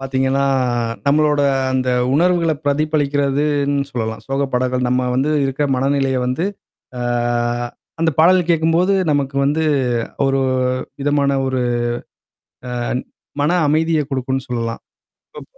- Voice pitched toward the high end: No, medium, 140 Hz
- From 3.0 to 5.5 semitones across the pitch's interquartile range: No, narrow, 2.4 semitones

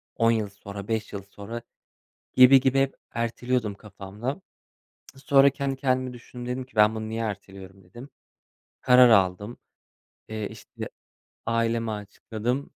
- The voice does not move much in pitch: No, average, 3.7 semitones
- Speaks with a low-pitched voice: Yes, low, 115 Hz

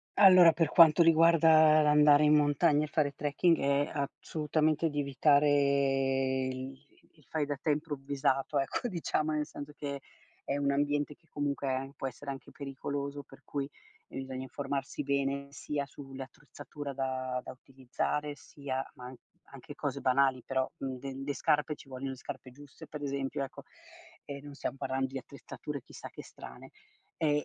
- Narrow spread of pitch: Yes, narrow, 1.7 semitones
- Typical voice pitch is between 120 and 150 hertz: Yes, medium, 140 Hz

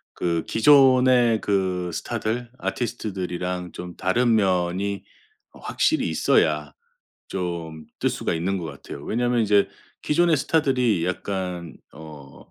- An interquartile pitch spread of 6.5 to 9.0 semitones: No, wide, 5.4 semitones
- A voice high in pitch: No, very low, 95 Hz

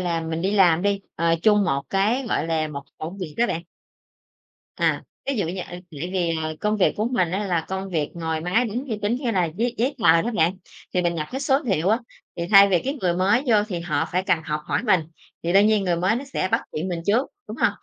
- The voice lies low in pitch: No, medium, 185 Hz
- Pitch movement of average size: Yes, average, 4.3 semitones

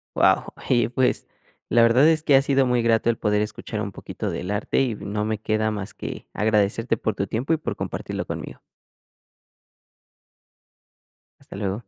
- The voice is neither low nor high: No, low, 110 Hz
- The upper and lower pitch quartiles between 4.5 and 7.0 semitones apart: No, average, 2.9 semitones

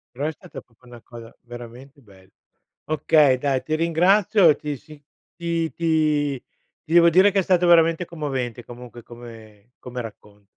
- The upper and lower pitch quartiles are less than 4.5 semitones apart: No, wide, 5.4 semitones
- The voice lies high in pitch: No, medium, 140 Hz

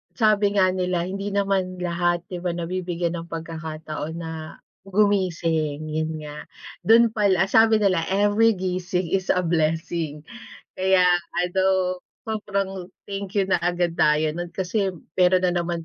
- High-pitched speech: No, medium, 180 Hz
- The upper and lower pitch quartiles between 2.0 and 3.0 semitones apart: Yes, average, 2.7 semitones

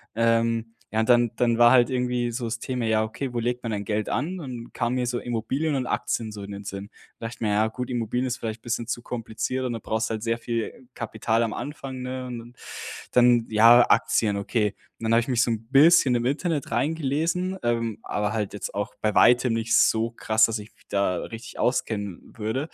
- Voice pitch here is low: Yes, low, 115 Hz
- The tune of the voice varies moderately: No, narrow, 2.2 semitones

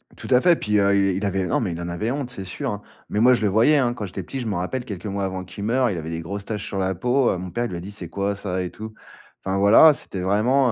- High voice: No, low, 100 Hz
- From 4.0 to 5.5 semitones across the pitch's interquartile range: Yes, average, 4.3 semitones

